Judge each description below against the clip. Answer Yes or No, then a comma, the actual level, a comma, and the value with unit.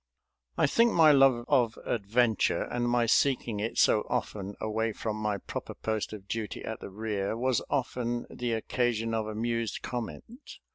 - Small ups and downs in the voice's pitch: Yes, narrow, 2.3 semitones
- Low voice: Yes, low, 115 Hz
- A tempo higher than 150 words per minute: Yes, average, 160 wpm